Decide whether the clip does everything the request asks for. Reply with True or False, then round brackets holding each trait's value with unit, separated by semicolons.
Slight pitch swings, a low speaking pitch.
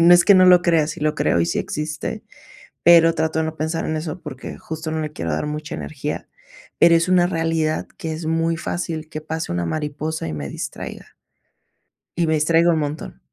False (1.5 semitones; 160 Hz)